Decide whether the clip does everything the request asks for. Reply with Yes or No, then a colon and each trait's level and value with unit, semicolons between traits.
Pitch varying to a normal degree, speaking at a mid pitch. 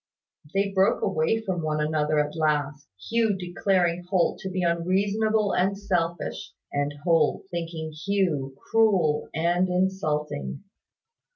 Yes: average, 3.9 semitones; medium, 175 Hz